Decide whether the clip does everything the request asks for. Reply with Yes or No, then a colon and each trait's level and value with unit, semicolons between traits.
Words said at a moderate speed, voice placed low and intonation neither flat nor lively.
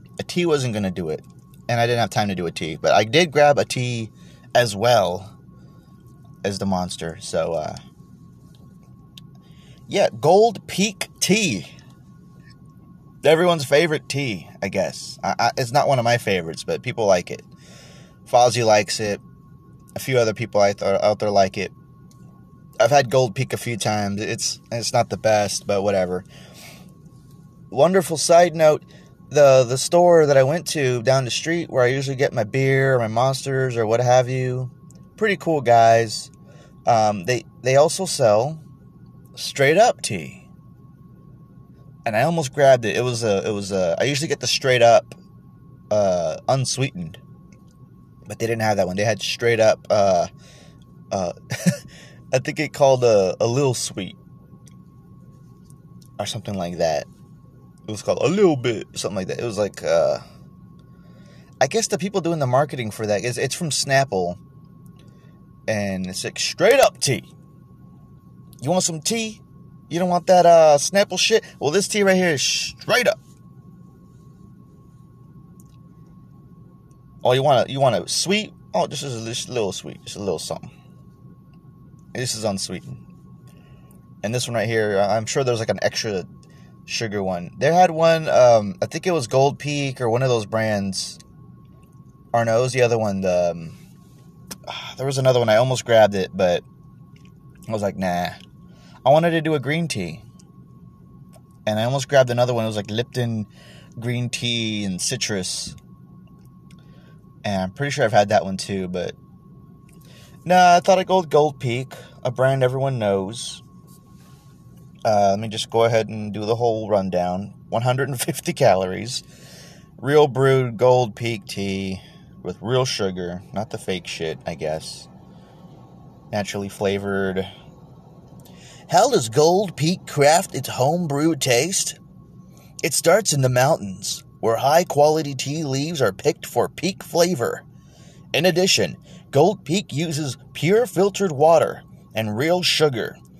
No: average, 160 wpm; low, 130 Hz; wide, 6.4 semitones